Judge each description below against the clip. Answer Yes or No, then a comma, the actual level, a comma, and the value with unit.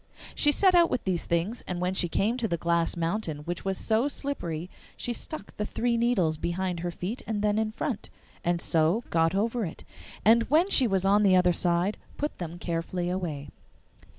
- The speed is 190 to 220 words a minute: Yes, average, 200 wpm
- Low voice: No, high, 190 Hz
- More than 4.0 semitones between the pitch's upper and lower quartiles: Yes, average, 5.1 semitones